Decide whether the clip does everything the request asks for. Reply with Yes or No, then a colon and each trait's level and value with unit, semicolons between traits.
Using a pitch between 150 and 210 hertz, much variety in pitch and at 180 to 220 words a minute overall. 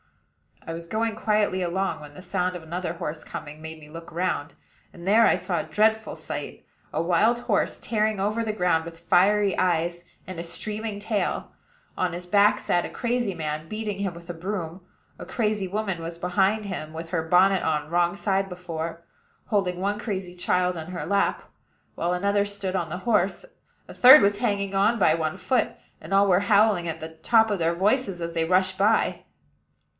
No: medium, 185 Hz; average, 3.5 semitones; average, 190 wpm